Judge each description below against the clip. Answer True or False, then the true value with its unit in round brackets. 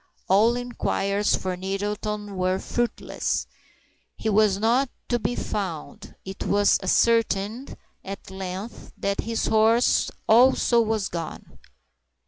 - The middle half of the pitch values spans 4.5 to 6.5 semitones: False (3.0 semitones)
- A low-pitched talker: False (210 Hz)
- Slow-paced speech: True (110 wpm)